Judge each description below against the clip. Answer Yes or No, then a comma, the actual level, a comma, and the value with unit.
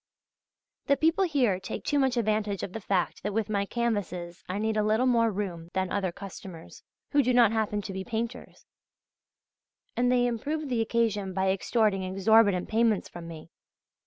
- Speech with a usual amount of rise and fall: Yes, average, 3.7 semitones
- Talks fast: No, average, 175 wpm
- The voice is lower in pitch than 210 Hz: No, high, 215 Hz